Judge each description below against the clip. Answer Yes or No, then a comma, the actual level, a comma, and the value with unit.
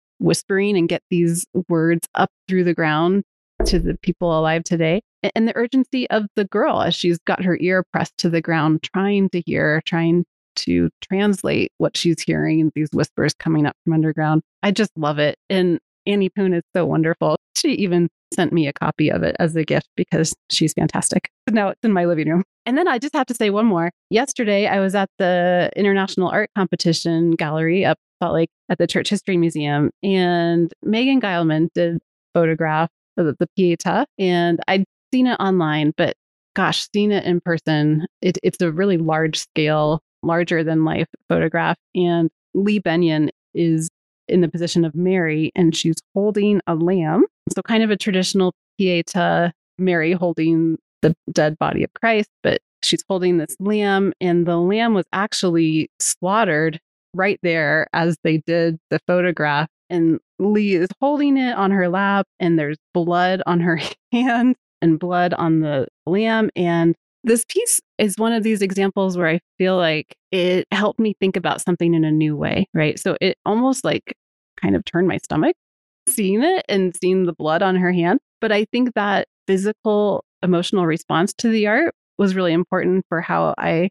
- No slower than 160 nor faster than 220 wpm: Yes, average, 180 wpm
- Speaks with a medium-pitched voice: Yes, medium, 180 Hz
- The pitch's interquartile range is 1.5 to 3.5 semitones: Yes, average, 3.2 semitones